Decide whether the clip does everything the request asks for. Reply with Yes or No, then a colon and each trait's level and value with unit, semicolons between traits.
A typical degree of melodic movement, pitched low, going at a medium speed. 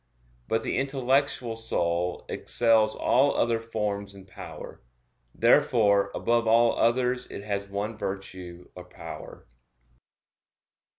No: average, 3.0 semitones; low, 110 Hz; slow, 110 wpm